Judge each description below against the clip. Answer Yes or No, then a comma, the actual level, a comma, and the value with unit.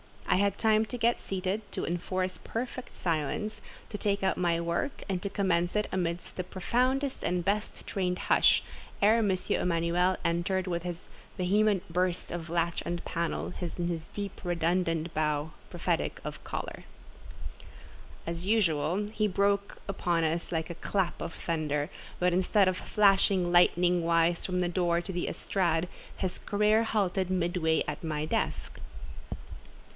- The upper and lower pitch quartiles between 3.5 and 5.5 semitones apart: No, average, 2.9 semitones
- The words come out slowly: No, average, 150 wpm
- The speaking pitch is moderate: Yes, medium, 180 Hz